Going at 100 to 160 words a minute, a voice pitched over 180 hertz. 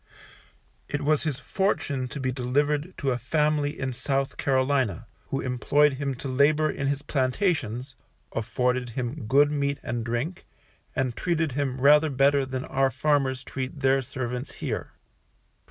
No: average, 150 wpm; low, 135 Hz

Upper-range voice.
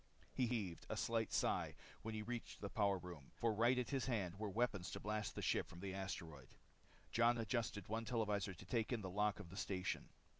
No: low, 105 Hz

